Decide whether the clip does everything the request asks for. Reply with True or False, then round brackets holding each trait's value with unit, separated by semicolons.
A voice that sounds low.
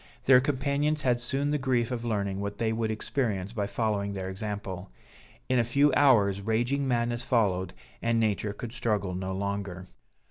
True (110 Hz)